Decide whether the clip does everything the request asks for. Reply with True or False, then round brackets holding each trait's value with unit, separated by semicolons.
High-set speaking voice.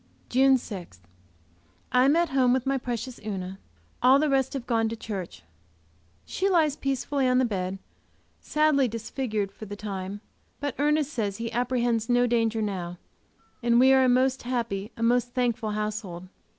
True (240 Hz)